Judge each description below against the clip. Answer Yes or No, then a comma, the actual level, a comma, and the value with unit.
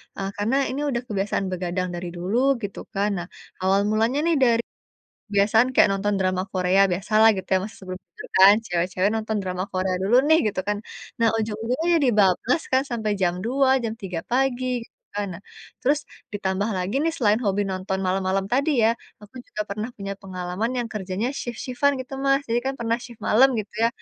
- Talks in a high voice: Yes, high, 205 Hz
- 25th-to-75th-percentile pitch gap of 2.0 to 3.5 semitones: No, average, 4.0 semitones